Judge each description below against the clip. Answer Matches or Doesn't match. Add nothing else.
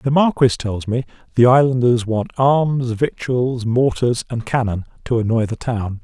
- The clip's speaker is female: Doesn't match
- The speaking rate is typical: Matches